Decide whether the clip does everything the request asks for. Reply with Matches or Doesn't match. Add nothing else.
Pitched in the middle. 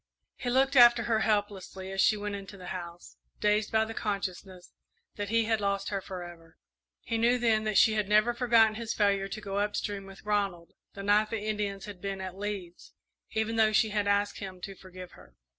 Doesn't match